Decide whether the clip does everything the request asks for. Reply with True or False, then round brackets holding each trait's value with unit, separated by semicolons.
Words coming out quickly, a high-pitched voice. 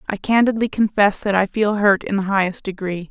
True (210 wpm; 200 Hz)